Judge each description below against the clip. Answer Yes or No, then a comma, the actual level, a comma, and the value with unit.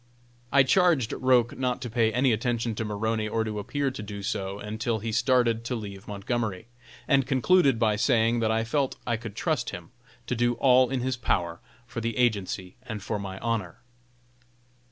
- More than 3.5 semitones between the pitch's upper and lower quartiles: No, average, 2.9 semitones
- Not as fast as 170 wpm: No, average, 185 wpm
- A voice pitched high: No, low, 115 Hz